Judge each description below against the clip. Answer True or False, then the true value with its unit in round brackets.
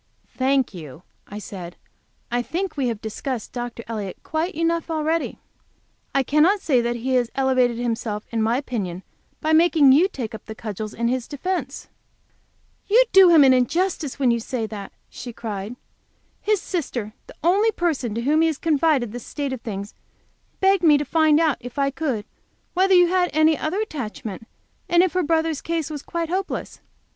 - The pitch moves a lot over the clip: True (6.0 semitones)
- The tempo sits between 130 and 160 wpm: False (175 wpm)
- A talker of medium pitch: False (275 Hz)